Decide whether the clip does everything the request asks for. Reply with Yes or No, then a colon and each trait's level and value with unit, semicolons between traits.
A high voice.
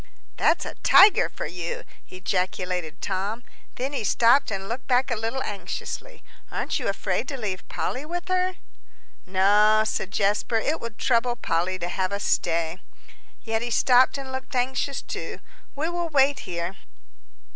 Yes: high, 225 Hz